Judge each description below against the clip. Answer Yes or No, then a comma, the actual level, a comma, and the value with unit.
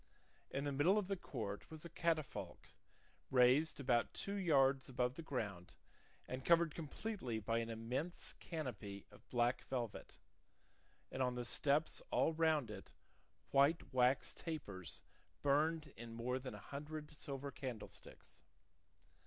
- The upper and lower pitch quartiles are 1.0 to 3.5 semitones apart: No, average, 4.2 semitones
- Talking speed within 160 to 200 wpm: No, slow, 135 wpm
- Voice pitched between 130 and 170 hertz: Yes, low, 135 Hz